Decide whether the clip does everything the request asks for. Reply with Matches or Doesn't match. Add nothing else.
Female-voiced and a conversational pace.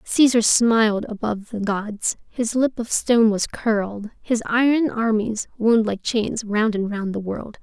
Matches